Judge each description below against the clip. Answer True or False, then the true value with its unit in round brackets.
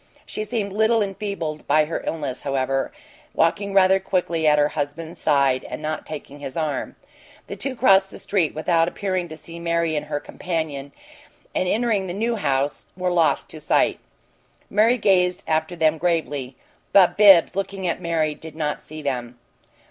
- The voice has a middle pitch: True (165 Hz)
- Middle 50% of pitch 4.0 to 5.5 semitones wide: True (4.3 semitones)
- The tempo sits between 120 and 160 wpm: False (170 wpm)